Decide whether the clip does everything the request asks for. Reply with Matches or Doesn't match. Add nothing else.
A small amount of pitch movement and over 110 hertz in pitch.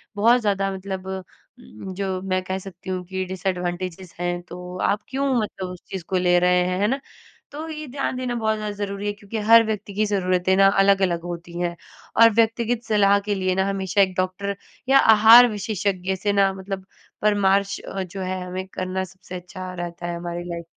Matches